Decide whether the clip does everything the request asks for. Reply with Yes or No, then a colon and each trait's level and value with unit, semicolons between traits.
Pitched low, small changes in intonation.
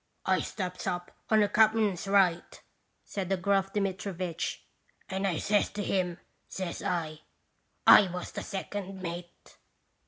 No: high, 190 Hz; narrow, 2.2 semitones